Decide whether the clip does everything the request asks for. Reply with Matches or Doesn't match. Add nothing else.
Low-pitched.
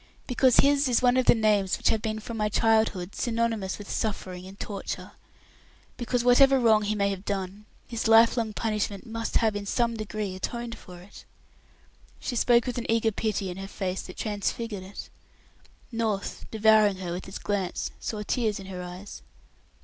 Doesn't match